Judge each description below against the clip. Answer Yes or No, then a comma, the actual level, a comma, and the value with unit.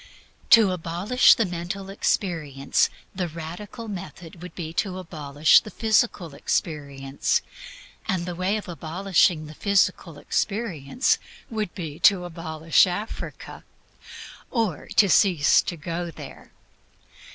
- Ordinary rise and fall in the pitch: Yes, average, 3.9 semitones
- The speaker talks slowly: Yes, slow, 120 wpm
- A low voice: No, medium, 175 Hz